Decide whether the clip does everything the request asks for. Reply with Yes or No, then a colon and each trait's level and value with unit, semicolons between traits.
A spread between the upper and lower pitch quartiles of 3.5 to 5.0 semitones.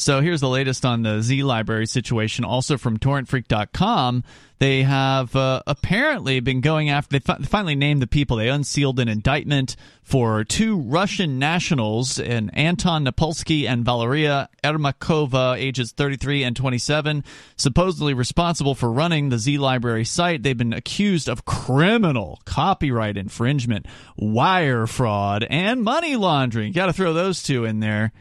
Yes: average, 3.9 semitones